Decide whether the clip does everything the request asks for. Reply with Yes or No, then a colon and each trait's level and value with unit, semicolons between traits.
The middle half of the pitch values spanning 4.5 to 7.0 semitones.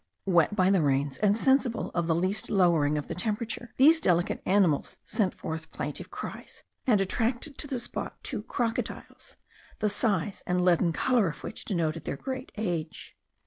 Yes: wide, 5.4 semitones